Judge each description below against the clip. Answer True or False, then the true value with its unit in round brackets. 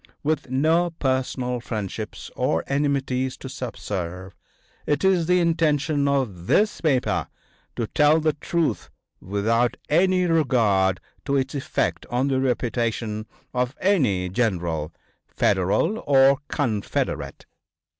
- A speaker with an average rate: False (115 wpm)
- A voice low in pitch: True (130 Hz)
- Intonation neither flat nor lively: False (5.7 semitones)